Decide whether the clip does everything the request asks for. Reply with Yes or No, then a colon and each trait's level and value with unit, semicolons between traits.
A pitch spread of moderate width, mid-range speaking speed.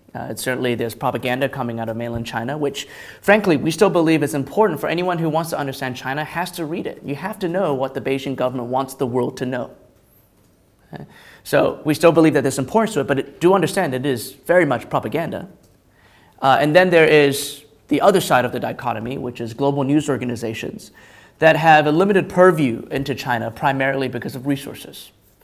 No: average, 4.1 semitones; fast, 210 wpm